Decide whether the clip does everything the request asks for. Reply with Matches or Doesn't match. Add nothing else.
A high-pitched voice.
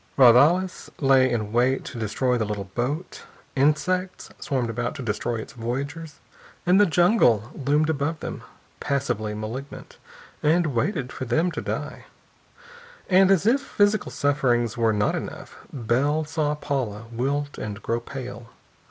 Doesn't match